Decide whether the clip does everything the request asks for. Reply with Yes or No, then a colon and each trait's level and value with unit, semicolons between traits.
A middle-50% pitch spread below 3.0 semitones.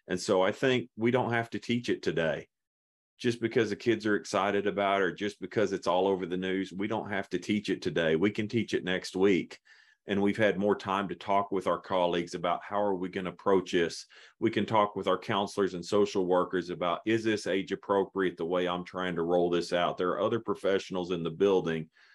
Yes: narrow, 2.4 semitones